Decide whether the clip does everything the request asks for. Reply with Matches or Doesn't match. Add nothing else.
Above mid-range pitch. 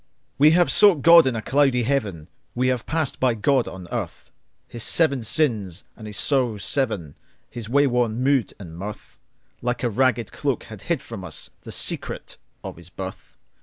Doesn't match